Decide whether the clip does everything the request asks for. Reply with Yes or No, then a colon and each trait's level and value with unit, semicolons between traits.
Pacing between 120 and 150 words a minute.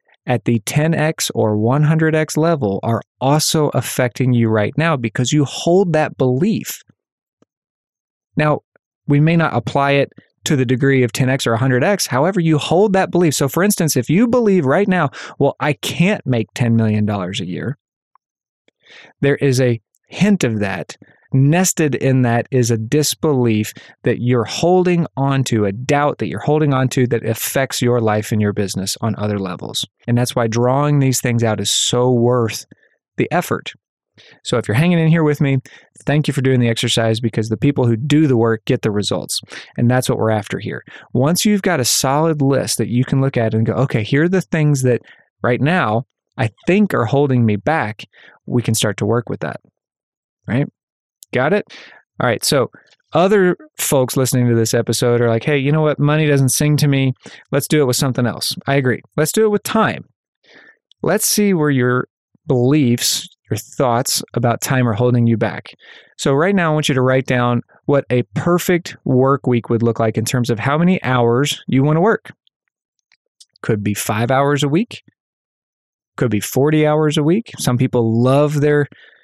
No: average, 190 wpm